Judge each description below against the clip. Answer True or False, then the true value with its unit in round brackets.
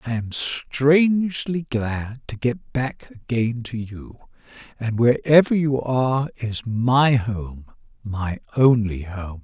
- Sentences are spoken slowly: True (120 wpm)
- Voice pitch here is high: False (120 Hz)